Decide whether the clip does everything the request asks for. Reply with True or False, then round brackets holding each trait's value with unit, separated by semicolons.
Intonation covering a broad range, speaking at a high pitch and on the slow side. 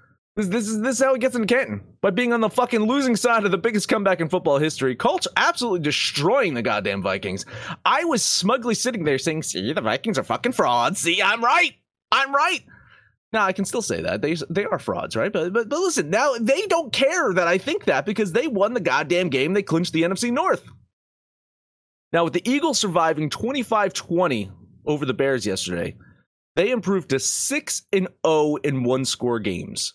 False (7.8 semitones; 200 Hz; 200 wpm)